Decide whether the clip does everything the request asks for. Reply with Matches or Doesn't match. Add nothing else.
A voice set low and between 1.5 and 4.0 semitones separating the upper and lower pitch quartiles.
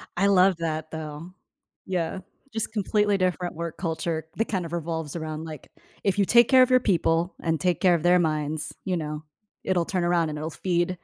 Doesn't match